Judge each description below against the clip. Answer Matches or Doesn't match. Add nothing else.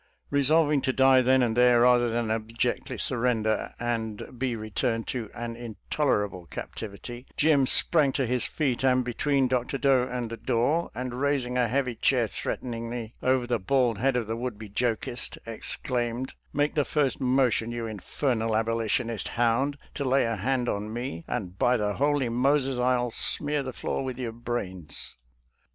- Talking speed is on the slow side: Doesn't match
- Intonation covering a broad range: Doesn't match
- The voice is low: Matches